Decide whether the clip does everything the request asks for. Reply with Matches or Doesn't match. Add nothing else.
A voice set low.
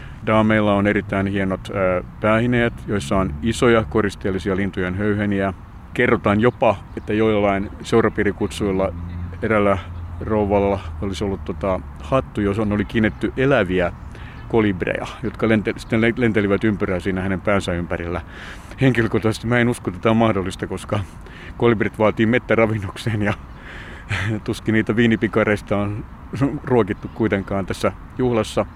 Matches